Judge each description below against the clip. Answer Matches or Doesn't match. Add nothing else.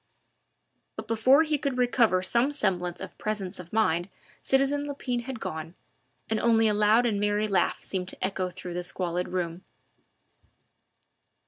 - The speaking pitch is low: Doesn't match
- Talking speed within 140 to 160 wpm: Matches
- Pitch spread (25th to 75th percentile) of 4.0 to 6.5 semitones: Matches